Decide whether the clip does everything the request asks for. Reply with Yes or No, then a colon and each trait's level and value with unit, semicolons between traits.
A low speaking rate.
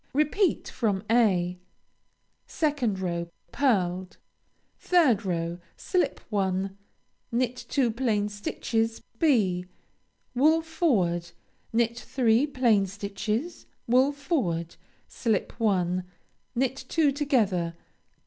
Yes: slow, 90 wpm